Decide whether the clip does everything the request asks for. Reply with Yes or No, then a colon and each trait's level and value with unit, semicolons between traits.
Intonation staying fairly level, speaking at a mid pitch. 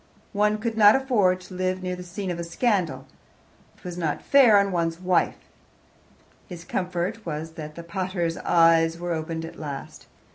No: average, 3.2 semitones; medium, 180 Hz